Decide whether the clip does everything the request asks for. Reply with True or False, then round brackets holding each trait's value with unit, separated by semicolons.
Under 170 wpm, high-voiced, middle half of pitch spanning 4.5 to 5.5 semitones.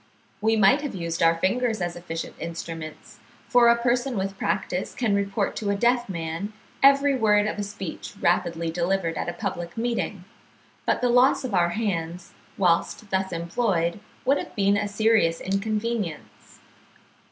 True (160 wpm; 200 Hz; 4.8 semitones)